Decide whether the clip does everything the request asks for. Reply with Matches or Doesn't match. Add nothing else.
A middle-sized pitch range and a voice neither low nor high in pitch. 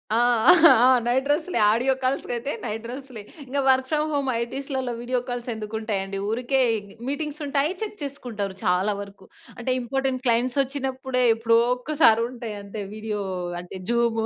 Doesn't match